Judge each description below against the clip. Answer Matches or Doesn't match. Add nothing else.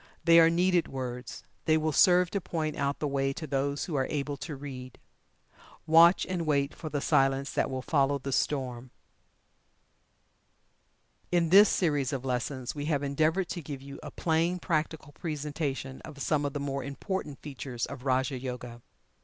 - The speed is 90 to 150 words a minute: Doesn't match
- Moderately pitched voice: Matches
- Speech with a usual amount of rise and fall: Matches